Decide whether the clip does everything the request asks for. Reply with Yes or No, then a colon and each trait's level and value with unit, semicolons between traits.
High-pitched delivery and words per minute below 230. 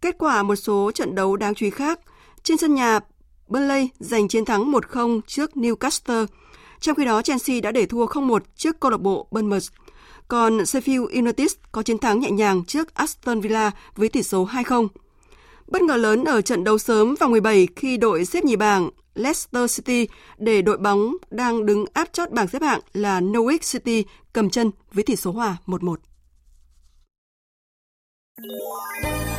Yes: high, 225 Hz; average, 170 wpm